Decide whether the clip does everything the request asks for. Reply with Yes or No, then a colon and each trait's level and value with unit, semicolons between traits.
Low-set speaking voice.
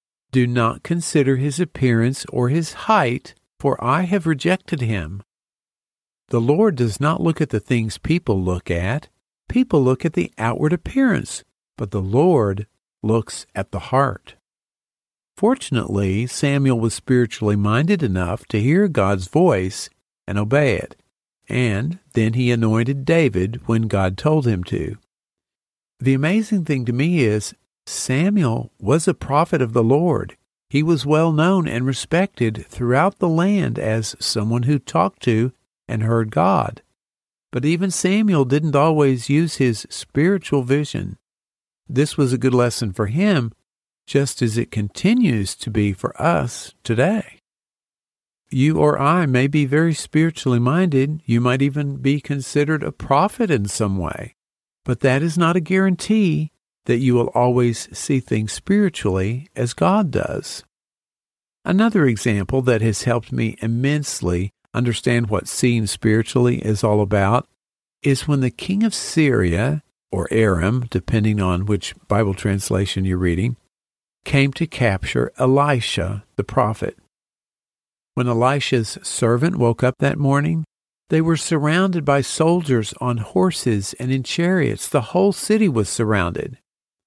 Yes: low, 130 Hz